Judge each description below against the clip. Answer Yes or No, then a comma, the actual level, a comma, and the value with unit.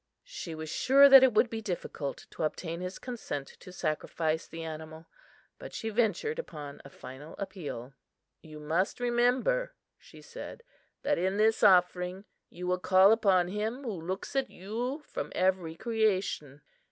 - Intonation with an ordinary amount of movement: No, wide, 6.3 semitones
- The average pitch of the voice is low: No, medium, 185 Hz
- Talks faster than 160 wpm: No, average, 155 wpm